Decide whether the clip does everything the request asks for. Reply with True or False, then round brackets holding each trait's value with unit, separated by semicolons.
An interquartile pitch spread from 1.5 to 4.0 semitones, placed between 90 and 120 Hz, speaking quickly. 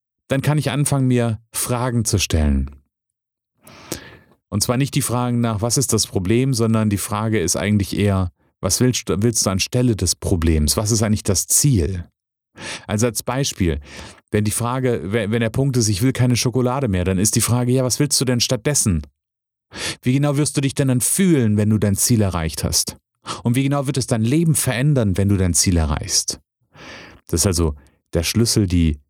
False (5.1 semitones; 115 Hz; 195 wpm)